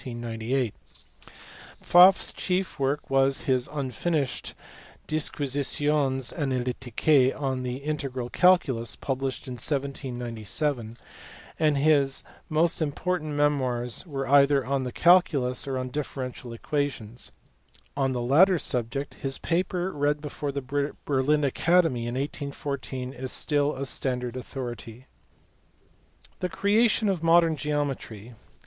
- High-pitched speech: No, medium, 140 Hz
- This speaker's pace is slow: Yes, slow, 110 wpm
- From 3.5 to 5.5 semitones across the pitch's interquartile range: No, average, 2.9 semitones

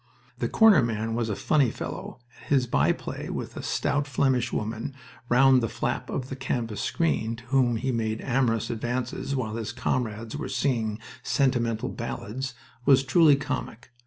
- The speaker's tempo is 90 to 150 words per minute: No, average, 165 wpm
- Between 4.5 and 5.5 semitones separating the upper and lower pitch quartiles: No, average, 2.9 semitones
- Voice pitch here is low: Yes, low, 120 Hz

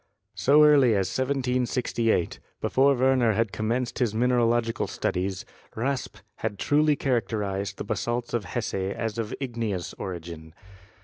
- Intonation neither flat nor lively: Yes, average, 4.0 semitones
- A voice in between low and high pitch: No, low, 115 Hz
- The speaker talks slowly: Yes, slow, 125 wpm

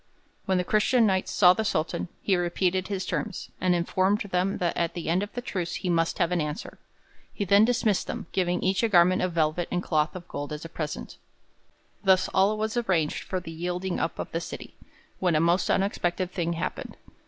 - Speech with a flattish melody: Yes, narrow, 2.2 semitones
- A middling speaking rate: No, fast, 210 wpm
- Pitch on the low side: No, medium, 180 Hz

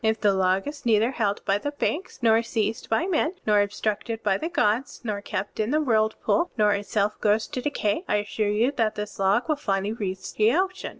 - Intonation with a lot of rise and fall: No, average, 3.8 semitones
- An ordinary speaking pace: No, fast, 215 wpm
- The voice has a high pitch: Yes, high, 220 Hz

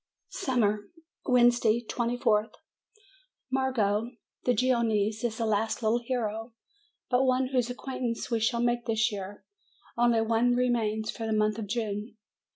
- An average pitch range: No, narrow, 2.1 semitones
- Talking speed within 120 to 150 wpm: Yes, slow, 135 wpm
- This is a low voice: No, high, 230 Hz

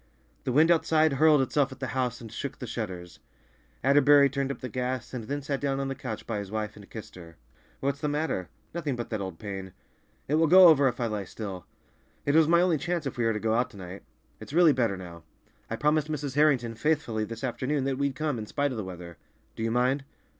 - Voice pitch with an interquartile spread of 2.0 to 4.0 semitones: No, average, 5.0 semitones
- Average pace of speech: No, fast, 235 wpm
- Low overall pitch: Yes, low, 130 Hz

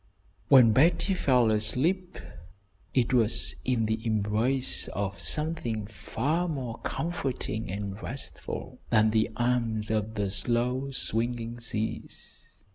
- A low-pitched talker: Yes, low, 115 Hz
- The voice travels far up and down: No, average, 3.4 semitones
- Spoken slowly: Yes, slow, 115 wpm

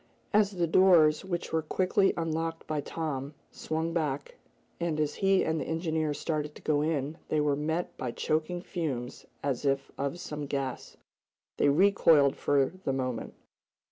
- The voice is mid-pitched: Yes, medium, 155 Hz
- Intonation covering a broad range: No, average, 2.8 semitones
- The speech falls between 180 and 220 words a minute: No, average, 160 wpm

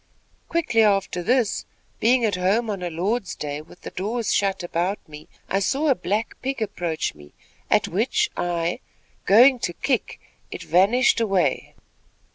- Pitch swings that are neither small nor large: Yes, average, 5.0 semitones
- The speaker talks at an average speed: Yes, average, 155 wpm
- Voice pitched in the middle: No, high, 200 Hz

